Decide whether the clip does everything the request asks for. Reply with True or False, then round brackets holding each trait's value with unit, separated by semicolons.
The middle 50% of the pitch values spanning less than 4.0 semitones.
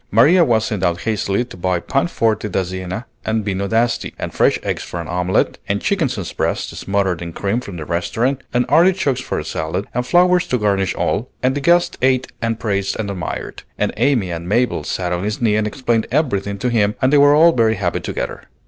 False (5.1 semitones)